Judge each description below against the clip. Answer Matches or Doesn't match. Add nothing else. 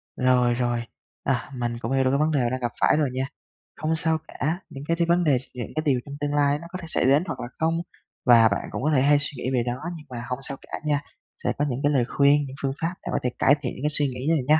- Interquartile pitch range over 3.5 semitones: Doesn't match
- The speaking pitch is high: Doesn't match